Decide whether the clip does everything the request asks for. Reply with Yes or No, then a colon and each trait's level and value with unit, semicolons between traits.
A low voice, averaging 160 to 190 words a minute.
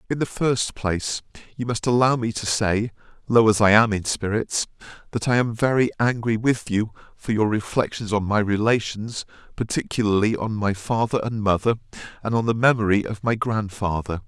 Yes: low, 110 Hz; average, 175 wpm